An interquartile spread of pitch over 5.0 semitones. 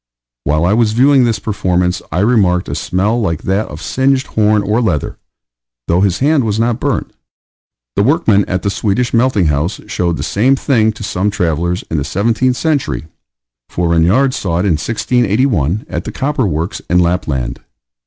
Yes: wide, 5.5 semitones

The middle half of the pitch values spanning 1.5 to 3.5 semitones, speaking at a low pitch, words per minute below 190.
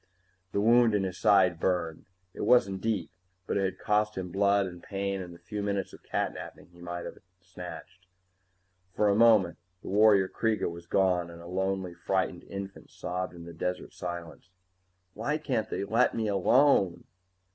Yes: average, 2.9 semitones; very low, 95 Hz; average, 175 wpm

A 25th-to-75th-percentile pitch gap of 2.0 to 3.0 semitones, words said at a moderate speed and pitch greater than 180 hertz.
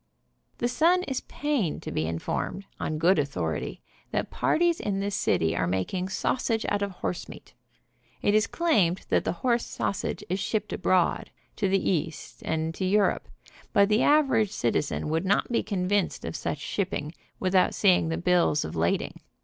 No: average, 4.8 semitones; average, 175 wpm; high, 190 Hz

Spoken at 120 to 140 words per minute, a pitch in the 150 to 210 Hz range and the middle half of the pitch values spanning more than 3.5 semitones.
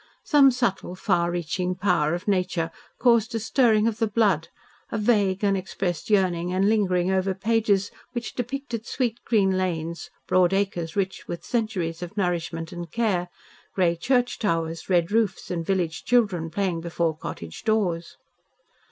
No: average, 150 wpm; high, 190 Hz; average, 4.1 semitones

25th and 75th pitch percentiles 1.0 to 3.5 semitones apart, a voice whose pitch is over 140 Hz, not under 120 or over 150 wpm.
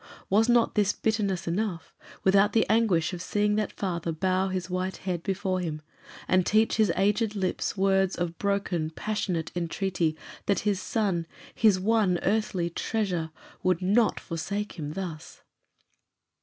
Yes: average, 3.0 semitones; high, 190 Hz; average, 145 wpm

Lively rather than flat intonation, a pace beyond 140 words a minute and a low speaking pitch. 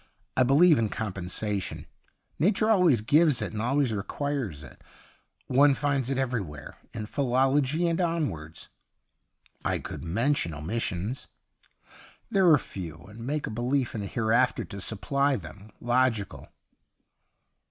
No: wide, 5.7 semitones; slow, 135 wpm; low, 125 Hz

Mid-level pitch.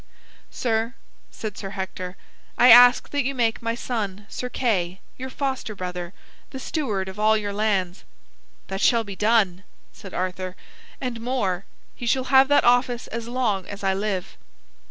No: high, 220 Hz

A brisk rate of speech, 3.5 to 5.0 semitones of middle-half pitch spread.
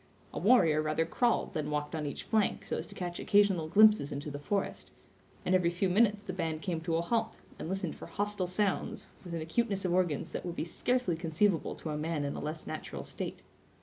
Yes: fast, 220 wpm; average, 4.3 semitones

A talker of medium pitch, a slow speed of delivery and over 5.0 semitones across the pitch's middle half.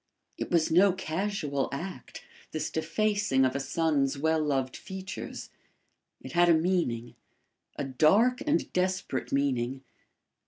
Yes: medium, 160 Hz; slow, 125 wpm; wide, 5.4 semitones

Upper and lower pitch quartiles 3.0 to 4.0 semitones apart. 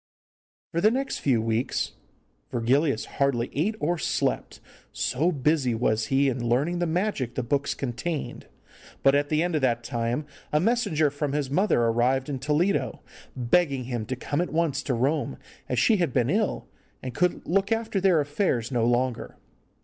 No: wide, 5.6 semitones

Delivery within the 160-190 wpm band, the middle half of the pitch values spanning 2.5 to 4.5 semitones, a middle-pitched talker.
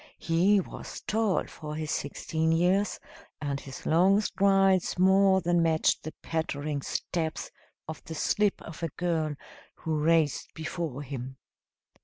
No: slow, 135 wpm; average, 3.5 semitones; medium, 165 Hz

